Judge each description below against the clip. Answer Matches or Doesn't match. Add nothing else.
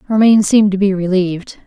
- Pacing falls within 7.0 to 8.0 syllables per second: Matches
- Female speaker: Matches